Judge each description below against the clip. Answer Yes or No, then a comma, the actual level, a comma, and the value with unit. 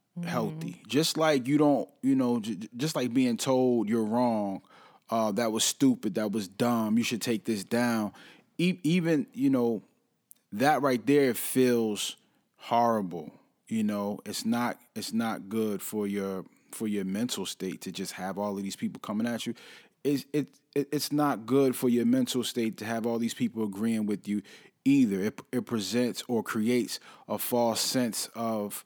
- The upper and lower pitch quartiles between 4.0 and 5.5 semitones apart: Yes, average, 4.5 semitones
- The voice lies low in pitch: Yes, low, 120 Hz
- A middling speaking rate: Yes, average, 175 wpm